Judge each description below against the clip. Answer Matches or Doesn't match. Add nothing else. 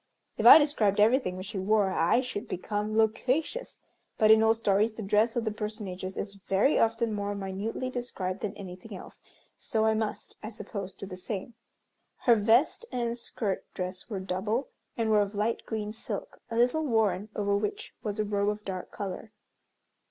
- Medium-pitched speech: Doesn't match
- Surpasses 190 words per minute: Doesn't match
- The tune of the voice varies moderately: Doesn't match